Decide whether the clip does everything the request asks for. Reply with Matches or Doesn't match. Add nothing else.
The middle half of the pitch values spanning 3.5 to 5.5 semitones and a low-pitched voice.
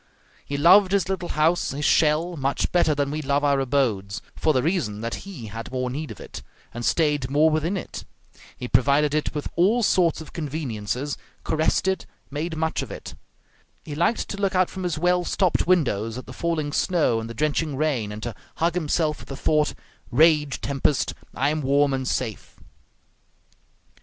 Doesn't match